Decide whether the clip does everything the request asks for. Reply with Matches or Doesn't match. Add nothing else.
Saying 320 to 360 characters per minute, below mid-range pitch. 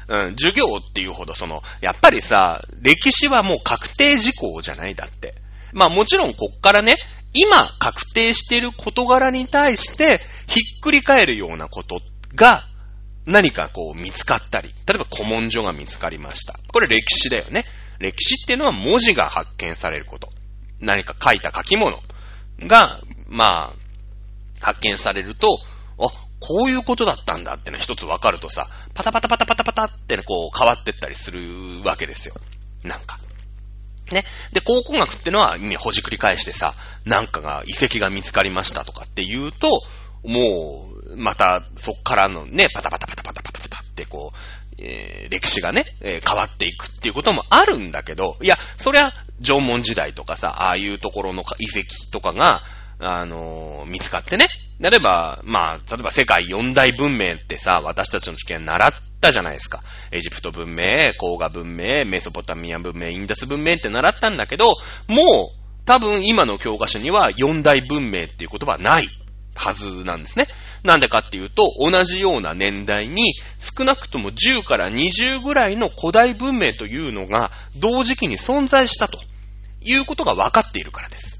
Matches